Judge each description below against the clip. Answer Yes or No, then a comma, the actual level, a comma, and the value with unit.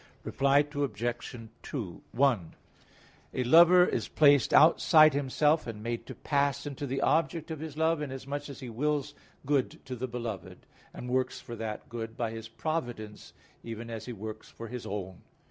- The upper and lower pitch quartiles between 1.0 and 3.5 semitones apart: No, average, 4.2 semitones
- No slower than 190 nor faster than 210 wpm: No, average, 165 wpm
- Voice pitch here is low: Yes, low, 130 Hz